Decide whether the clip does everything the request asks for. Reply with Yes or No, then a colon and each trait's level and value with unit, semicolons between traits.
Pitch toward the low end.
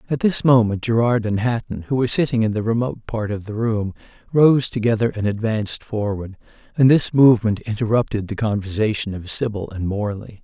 Yes: low, 110 Hz